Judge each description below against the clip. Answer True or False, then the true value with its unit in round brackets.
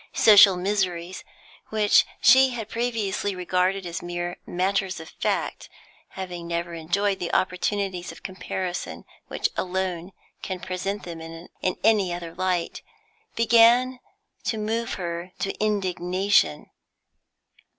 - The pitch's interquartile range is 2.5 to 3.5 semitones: True (2.8 semitones)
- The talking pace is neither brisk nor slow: False (115 wpm)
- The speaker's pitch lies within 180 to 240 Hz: True (185 Hz)